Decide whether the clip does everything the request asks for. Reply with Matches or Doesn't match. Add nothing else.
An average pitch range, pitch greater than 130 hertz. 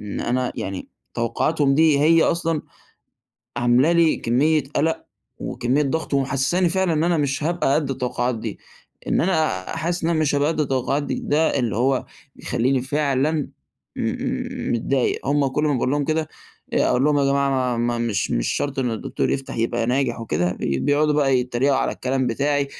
Matches